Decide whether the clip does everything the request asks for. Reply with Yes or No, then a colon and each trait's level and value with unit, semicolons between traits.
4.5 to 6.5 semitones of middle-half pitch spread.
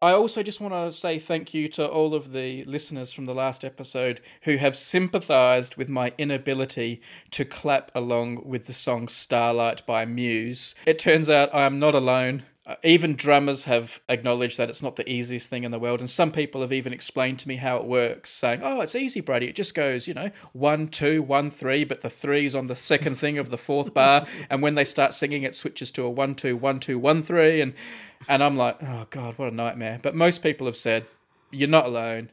No: average, 3.4 semitones